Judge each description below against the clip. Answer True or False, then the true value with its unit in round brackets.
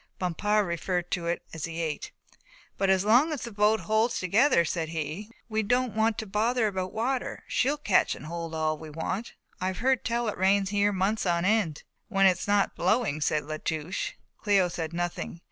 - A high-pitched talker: True (195 Hz)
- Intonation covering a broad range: False (4.4 semitones)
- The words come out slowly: False (195 wpm)